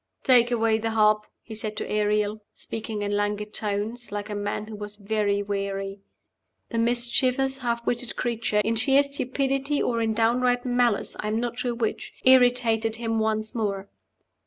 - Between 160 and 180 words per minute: Yes, average, 165 wpm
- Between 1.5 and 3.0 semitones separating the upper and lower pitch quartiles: Yes, narrow, 2.6 semitones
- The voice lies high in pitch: Yes, high, 225 Hz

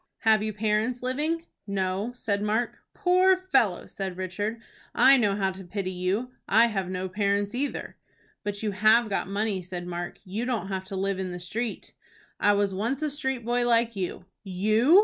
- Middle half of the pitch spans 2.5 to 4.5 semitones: Yes, average, 4.0 semitones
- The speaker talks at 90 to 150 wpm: No, average, 185 wpm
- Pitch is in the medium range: No, high, 210 Hz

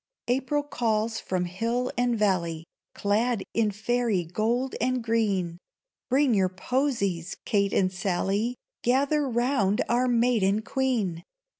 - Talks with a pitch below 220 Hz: No, high, 225 Hz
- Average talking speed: No, slow, 120 wpm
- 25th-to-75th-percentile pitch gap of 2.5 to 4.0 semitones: No, average, 4.4 semitones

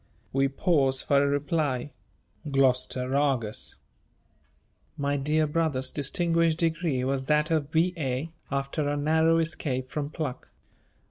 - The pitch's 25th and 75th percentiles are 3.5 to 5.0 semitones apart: No, average, 2.9 semitones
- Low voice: No, medium, 145 Hz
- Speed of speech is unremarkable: No, slow, 120 wpm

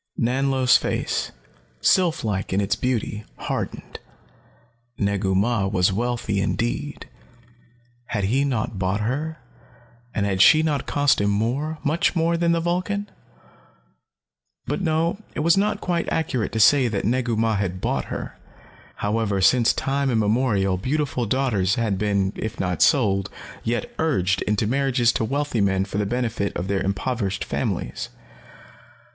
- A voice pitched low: Yes, low, 115 Hz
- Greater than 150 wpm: No, average, 145 wpm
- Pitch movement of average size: No, wide, 5.9 semitones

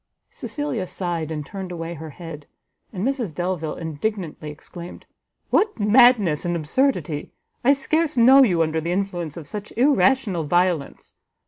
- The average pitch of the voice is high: No, medium, 180 Hz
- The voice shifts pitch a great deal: Yes, wide, 6.7 semitones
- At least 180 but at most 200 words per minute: No, average, 140 wpm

